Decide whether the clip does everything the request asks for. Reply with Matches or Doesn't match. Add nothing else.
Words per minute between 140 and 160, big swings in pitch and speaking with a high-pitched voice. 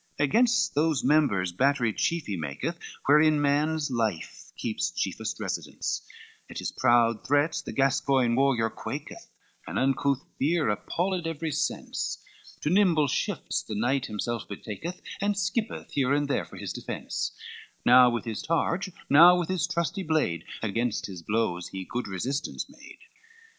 Doesn't match